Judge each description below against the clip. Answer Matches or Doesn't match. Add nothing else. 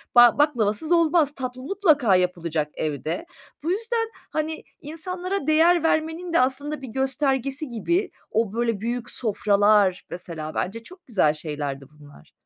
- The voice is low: Doesn't match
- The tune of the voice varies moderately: Doesn't match